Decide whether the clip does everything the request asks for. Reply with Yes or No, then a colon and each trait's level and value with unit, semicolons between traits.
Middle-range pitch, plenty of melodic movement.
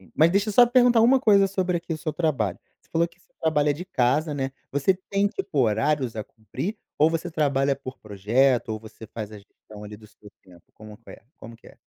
Yes: medium, 145 Hz; wide, 8.3 semitones